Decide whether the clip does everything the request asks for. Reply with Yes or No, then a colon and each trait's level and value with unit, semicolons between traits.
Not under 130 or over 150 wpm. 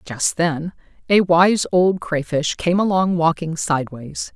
Yes: average, 140 wpm